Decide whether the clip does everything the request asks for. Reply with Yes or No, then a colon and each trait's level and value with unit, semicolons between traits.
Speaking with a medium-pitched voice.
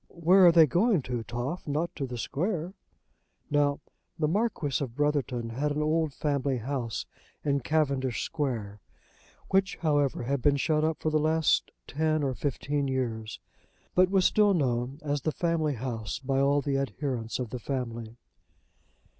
Yes: medium, 145 Hz